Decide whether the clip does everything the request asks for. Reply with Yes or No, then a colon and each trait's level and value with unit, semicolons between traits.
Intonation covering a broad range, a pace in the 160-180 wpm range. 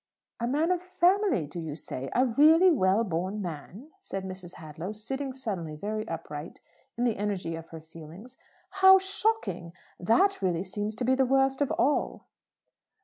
Yes: wide, 8.2 semitones; average, 165 wpm